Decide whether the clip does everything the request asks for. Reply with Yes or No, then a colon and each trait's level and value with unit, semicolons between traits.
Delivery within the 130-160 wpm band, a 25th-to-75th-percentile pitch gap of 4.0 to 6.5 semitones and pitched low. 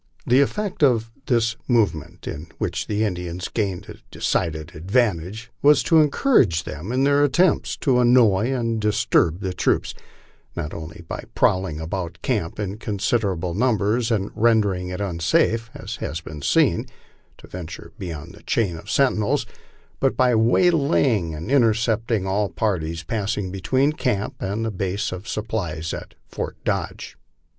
Yes: average, 150 wpm; average, 5.2 semitones; low, 105 Hz